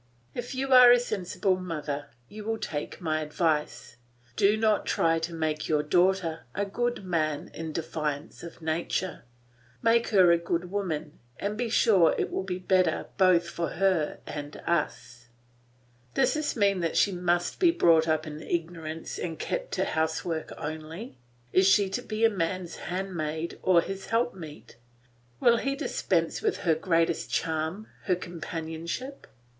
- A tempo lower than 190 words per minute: Yes, average, 155 wpm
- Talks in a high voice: No, medium, 175 Hz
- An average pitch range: Yes, average, 4.0 semitones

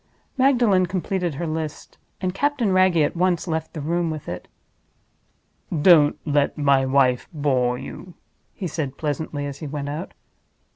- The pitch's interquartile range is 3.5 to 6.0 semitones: Yes, average, 4.2 semitones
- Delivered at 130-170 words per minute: Yes, average, 150 wpm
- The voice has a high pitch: No, medium, 160 Hz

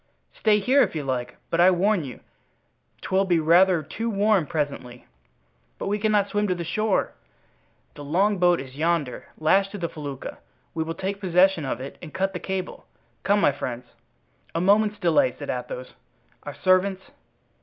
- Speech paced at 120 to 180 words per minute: Yes, average, 170 wpm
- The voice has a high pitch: No, medium, 180 Hz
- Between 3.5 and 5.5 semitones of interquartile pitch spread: Yes, average, 4.4 semitones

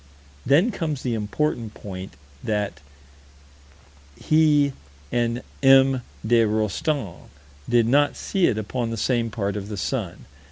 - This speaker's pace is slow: Yes, slow, 125 wpm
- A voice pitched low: Yes, low, 120 Hz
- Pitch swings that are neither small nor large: Yes, average, 4.8 semitones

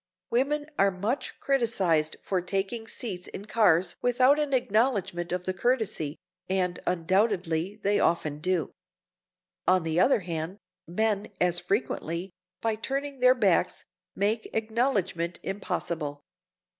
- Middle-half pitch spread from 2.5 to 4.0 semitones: No, average, 4.8 semitones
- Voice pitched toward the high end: Yes, high, 195 Hz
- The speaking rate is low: Yes, slow, 120 wpm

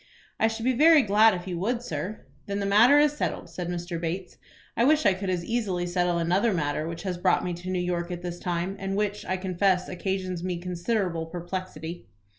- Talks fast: Yes, fast, 215 wpm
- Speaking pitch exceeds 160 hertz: Yes, medium, 185 Hz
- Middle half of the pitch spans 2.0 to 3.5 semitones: Yes, average, 2.8 semitones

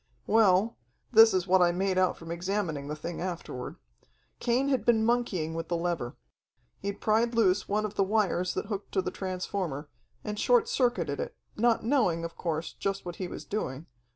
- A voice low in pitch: No, high, 190 Hz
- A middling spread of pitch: Yes, average, 4.3 semitones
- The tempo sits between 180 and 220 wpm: Yes, average, 185 wpm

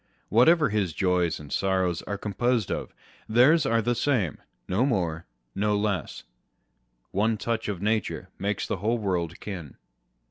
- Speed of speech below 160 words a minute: Yes, average, 150 wpm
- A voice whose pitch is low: Yes, low, 105 Hz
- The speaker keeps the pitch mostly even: No, average, 4.0 semitones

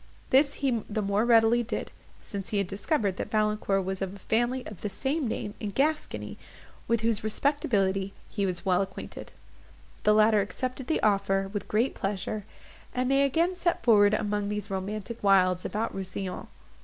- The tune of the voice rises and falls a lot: No, average, 3.4 semitones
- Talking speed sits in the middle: Yes, average, 170 wpm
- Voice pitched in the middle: No, high, 210 Hz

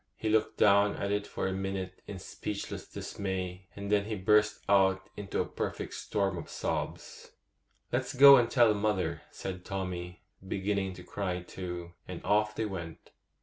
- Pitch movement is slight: Yes, narrow, 2.1 semitones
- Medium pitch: No, very low, 95 Hz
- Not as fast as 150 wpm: No, average, 165 wpm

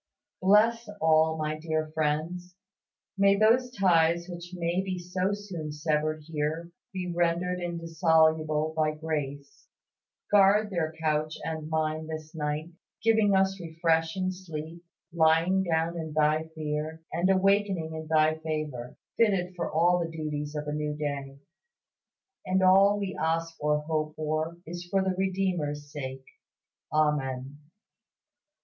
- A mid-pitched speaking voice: Yes, medium, 160 Hz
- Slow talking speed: Yes, slow, 130 wpm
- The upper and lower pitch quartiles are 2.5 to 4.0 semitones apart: Yes, average, 2.8 semitones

